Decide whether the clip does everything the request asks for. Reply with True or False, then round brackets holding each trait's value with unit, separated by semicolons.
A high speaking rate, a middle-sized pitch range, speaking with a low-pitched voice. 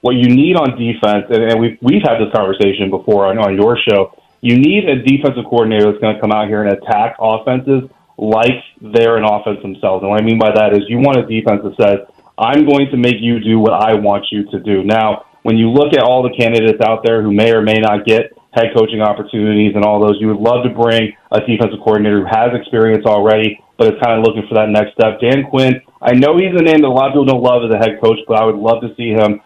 False (255 wpm; 2.2 semitones; 110 Hz)